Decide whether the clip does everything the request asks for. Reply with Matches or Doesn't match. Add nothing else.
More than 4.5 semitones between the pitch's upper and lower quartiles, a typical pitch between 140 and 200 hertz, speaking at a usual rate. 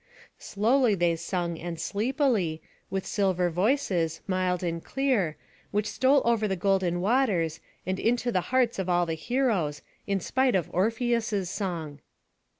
Matches